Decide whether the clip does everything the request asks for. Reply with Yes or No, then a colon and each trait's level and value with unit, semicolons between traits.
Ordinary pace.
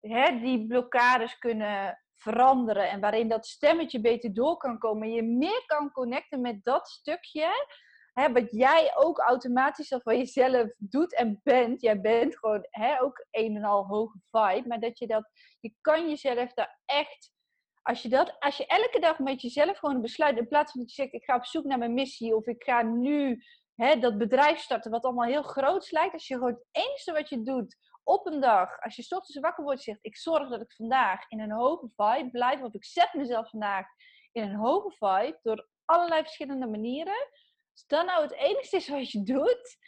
No: fast, 205 wpm